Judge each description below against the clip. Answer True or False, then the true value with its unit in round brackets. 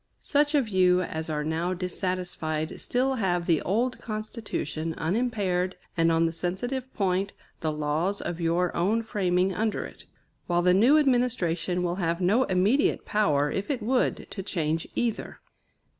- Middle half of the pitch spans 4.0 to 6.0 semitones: True (4.7 semitones)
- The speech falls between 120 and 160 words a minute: True (155 wpm)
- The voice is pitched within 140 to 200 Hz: True (185 Hz)